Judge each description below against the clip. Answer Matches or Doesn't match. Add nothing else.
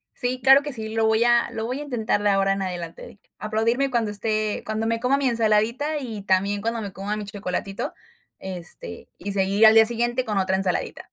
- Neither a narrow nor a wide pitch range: Matches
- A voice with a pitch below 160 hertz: Doesn't match